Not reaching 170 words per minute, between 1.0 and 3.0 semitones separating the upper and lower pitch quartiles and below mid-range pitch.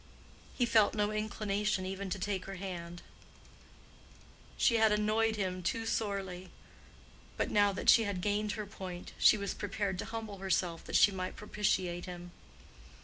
No: average, 155 wpm; narrow, 2.4 semitones; high, 200 Hz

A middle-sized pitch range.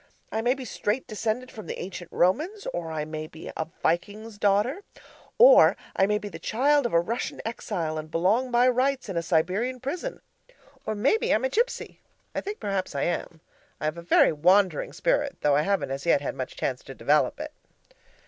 No: wide, 7.1 semitones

